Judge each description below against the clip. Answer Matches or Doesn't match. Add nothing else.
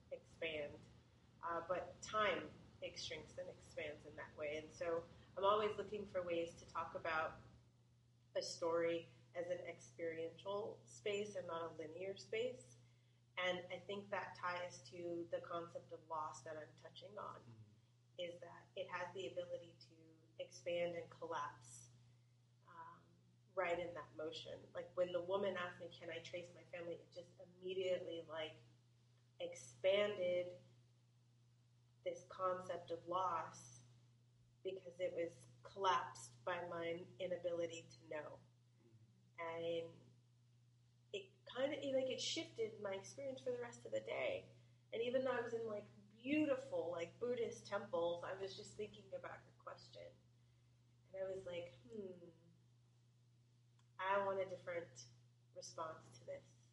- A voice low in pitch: Doesn't match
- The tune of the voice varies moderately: Doesn't match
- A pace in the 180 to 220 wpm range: Doesn't match